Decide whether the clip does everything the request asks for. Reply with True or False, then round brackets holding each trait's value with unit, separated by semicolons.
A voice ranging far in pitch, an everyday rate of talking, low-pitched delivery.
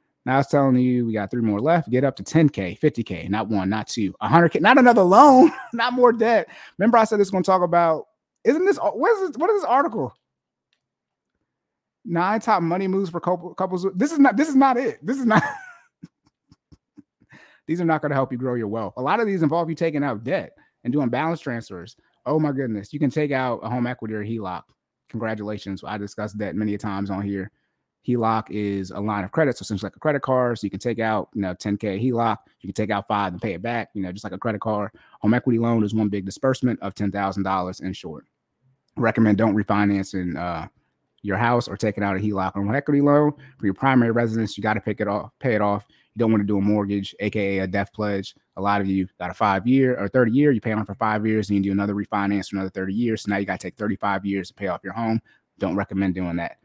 False (6.2 semitones; 250 wpm; 110 Hz)